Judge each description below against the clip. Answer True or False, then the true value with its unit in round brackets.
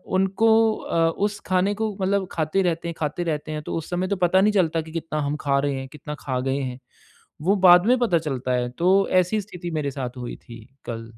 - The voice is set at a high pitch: False (165 Hz)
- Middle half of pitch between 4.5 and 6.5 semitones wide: True (5.2 semitones)